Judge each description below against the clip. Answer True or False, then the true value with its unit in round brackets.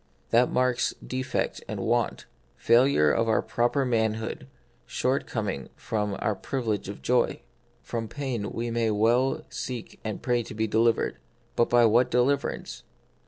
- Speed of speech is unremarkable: True (145 wpm)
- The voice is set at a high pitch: False (115 Hz)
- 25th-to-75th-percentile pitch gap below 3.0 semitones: True (2.4 semitones)